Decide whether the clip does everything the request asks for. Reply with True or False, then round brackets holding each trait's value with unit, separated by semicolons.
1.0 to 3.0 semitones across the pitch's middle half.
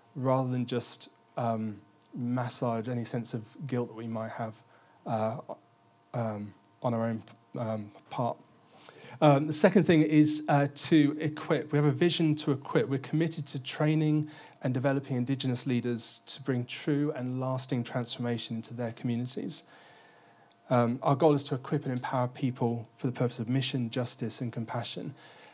False (3.8 semitones)